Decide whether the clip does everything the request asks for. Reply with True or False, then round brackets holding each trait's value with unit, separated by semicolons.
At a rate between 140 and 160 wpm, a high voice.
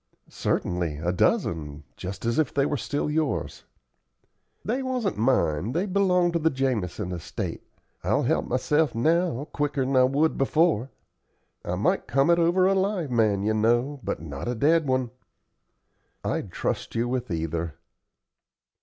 False (150 wpm; 130 Hz)